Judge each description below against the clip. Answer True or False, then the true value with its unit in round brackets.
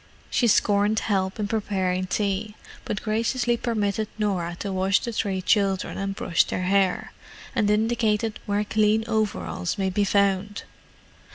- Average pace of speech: True (145 wpm)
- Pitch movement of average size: False (2.2 semitones)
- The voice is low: False (205 Hz)